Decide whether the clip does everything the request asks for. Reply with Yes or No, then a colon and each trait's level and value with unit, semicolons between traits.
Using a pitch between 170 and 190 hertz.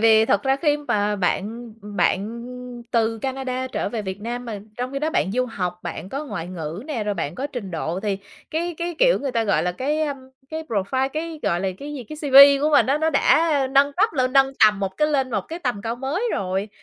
No: very high, 250 Hz